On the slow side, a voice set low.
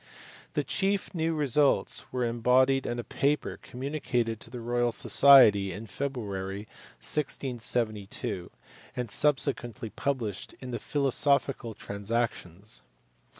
Yes: slow, 110 wpm; low, 120 Hz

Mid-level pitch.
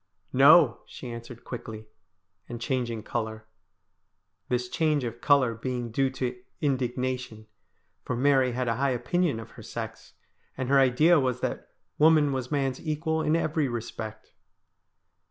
No: low, 125 Hz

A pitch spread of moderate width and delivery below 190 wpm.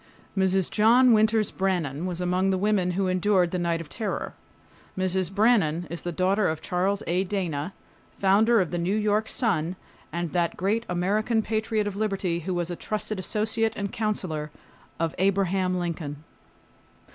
Yes: average, 3.2 semitones; average, 160 wpm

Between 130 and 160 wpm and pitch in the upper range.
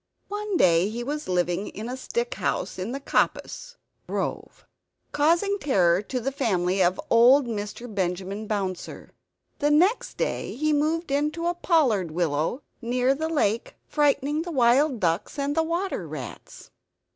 Yes: average, 145 wpm; very high, 255 Hz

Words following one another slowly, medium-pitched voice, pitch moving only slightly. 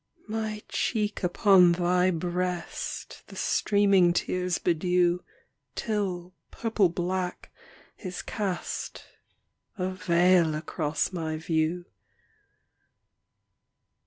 Yes: slow, 80 wpm; medium, 180 Hz; narrow, 1.8 semitones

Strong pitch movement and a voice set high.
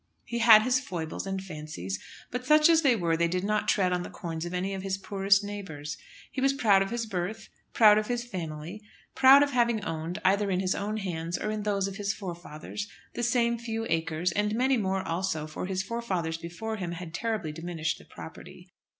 No: average, 4.6 semitones; high, 195 Hz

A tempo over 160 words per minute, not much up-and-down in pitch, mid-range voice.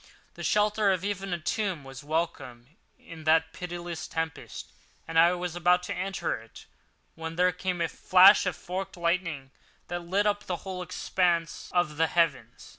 Yes: average, 170 wpm; narrow, 2.2 semitones; medium, 175 Hz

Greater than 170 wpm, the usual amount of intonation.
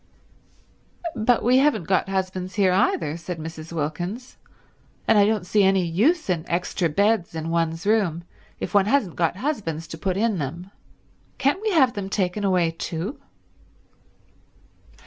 No: average, 150 wpm; average, 4.4 semitones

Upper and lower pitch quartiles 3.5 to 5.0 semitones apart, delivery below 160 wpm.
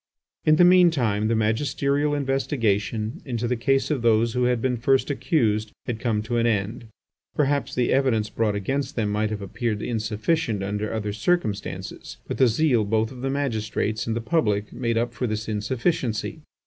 No: average, 3.9 semitones; average, 180 wpm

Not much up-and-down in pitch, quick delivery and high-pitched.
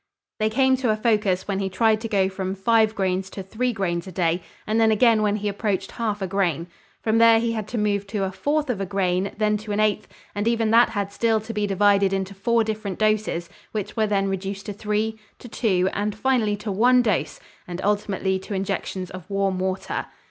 Yes: narrow, 2.3 semitones; fast, 220 wpm; high, 205 Hz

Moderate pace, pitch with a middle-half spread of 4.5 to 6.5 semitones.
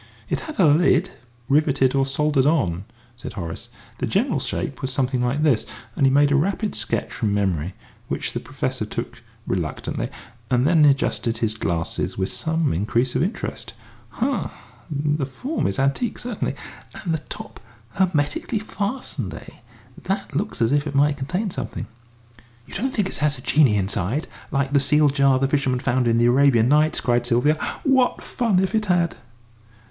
Yes: average, 175 wpm; average, 5.2 semitones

